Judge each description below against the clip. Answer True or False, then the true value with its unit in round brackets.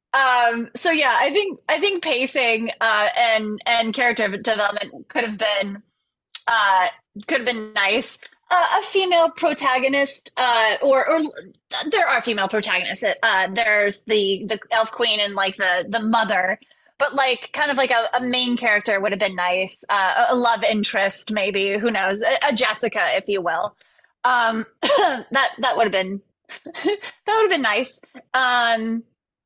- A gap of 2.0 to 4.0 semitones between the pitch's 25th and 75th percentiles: False (4.7 semitones)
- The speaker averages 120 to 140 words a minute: False (165 wpm)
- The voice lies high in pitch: True (235 Hz)